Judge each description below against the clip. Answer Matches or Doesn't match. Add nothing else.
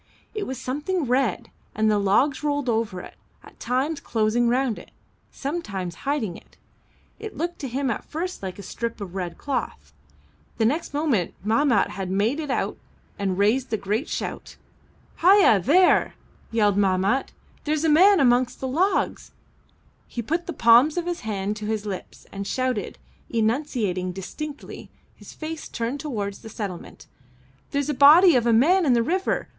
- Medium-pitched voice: Doesn't match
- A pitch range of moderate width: Doesn't match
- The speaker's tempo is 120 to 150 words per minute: Doesn't match